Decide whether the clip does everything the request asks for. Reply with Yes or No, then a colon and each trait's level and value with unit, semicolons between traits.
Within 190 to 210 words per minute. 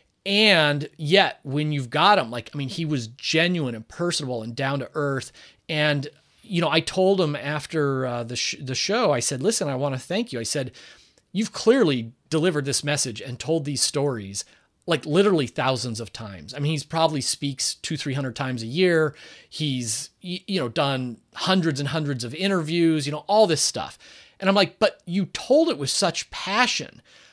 Yes: average, 195 wpm